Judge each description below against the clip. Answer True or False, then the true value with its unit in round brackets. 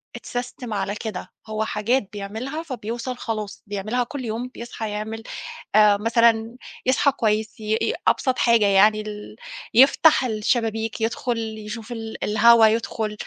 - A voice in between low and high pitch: False (225 Hz)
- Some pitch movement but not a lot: False (2.1 semitones)